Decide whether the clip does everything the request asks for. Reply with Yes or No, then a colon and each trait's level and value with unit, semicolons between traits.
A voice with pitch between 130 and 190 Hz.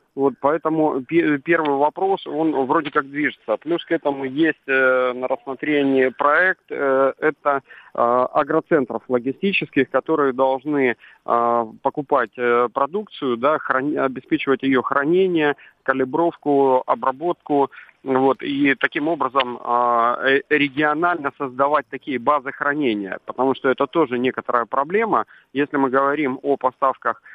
Yes: medium, 140 Hz